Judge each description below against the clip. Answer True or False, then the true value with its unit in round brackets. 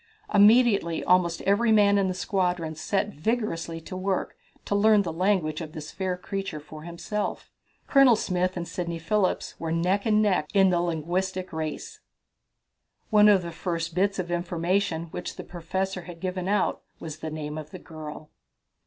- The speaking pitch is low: False (180 Hz)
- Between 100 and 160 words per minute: False (170 wpm)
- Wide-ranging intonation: False (3.3 semitones)